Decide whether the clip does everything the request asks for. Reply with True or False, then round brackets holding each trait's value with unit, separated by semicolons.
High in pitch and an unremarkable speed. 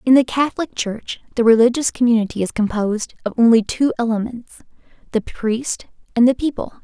True (235 Hz; 160 wpm)